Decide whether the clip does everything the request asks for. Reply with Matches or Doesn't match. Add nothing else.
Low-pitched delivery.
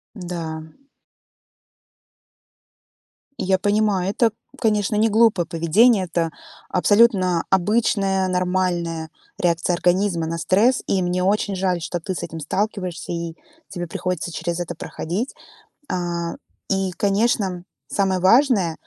Doesn't match